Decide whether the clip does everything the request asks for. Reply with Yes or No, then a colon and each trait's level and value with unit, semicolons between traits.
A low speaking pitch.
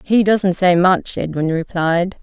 No: medium, 180 Hz